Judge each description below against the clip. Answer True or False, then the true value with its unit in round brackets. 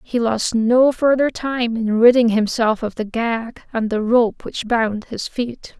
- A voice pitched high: True (230 Hz)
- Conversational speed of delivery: True (185 wpm)